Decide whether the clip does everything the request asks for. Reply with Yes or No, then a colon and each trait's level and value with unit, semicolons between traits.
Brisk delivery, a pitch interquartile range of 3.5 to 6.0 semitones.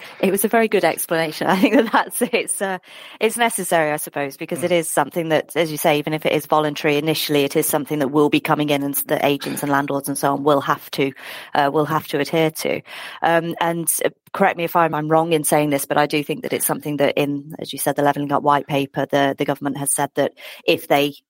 No: fast, 255 wpm; average, 2.7 semitones